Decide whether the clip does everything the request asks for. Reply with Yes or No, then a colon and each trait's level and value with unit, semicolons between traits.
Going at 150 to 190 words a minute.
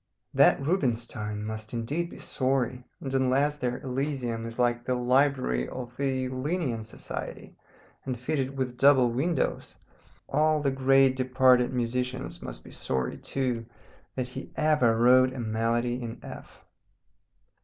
No: slow, 135 wpm